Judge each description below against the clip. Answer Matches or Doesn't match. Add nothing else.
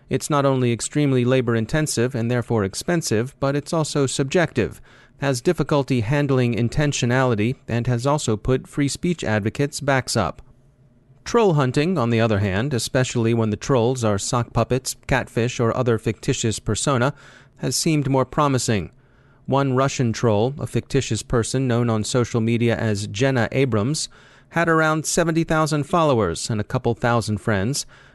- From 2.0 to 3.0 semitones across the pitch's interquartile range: Doesn't match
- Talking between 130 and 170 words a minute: Matches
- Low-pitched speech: Matches